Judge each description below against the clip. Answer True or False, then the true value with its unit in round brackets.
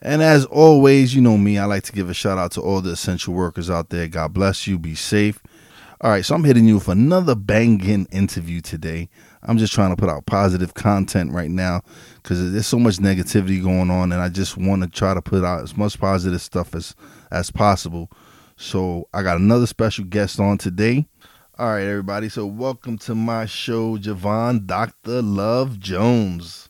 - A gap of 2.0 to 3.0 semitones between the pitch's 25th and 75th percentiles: False (3.7 semitones)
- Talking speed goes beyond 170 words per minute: True (200 wpm)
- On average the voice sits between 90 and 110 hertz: True (100 Hz)